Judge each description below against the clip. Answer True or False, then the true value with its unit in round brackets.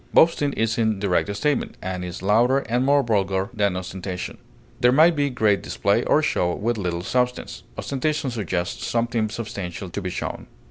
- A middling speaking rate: True (170 wpm)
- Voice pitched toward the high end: False (110 Hz)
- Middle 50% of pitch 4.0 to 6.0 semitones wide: True (4.8 semitones)